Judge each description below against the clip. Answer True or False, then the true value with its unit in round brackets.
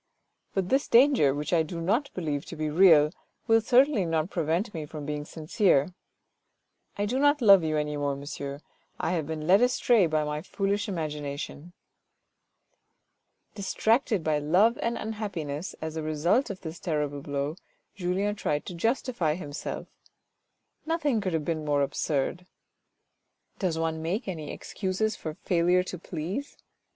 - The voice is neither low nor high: True (170 Hz)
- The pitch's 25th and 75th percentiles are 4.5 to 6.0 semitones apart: True (5.2 semitones)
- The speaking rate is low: False (150 wpm)